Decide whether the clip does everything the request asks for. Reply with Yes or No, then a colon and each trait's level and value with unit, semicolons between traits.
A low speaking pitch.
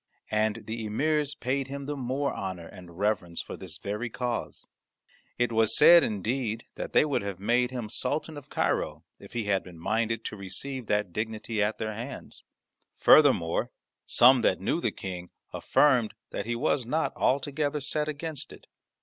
Yes: low, 115 Hz